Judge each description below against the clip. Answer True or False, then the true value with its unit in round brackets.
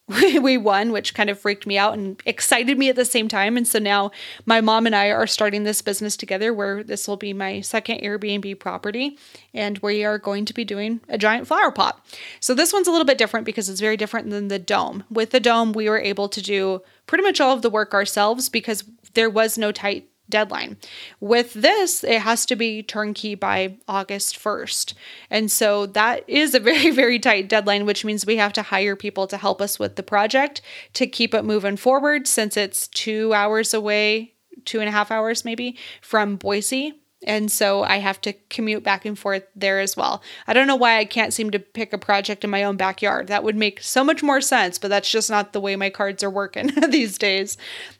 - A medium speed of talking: False (220 wpm)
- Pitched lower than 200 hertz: False (215 Hz)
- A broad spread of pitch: False (2.4 semitones)